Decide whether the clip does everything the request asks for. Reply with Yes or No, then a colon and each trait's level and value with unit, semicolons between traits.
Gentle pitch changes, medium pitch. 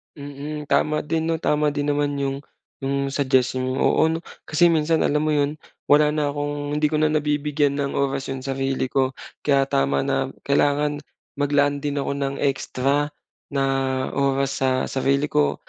Yes: narrow, 1.4 semitones; medium, 145 Hz